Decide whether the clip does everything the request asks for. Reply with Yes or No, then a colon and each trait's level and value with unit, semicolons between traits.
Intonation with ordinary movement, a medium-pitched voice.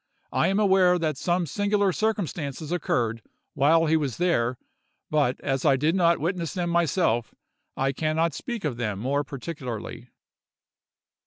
Yes: average, 4.9 semitones; medium, 155 Hz